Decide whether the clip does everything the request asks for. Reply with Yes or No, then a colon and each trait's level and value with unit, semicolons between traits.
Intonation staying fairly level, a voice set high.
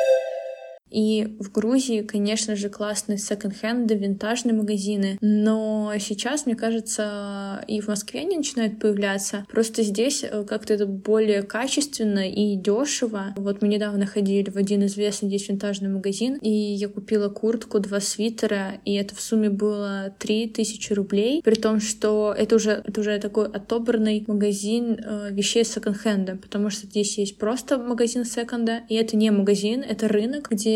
Yes: narrow, 1.6 semitones; high, 210 Hz